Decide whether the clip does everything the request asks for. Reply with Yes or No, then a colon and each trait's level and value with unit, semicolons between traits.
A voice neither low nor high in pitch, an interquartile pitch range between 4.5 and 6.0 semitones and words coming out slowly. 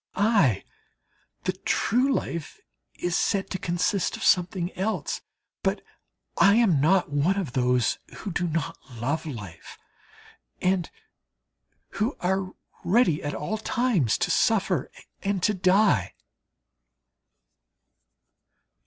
Yes: medium, 180 Hz; average, 5.1 semitones; slow, 110 wpm